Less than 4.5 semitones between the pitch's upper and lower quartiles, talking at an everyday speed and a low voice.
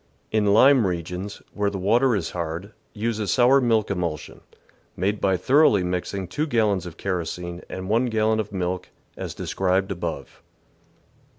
Yes: average, 3.5 semitones; average, 160 wpm; low, 100 Hz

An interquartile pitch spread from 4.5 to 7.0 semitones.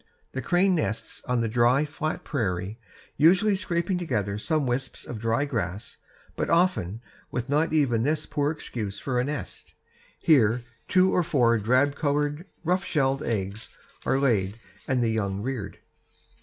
Yes: wide, 5.5 semitones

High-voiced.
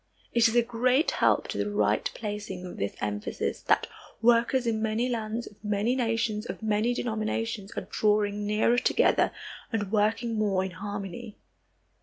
Yes: high, 215 Hz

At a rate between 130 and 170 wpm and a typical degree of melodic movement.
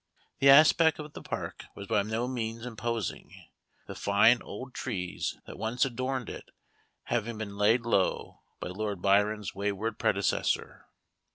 Yes: average, 145 wpm; average, 3.5 semitones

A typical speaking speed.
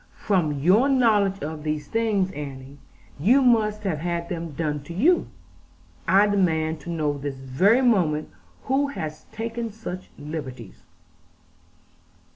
No: slow, 130 wpm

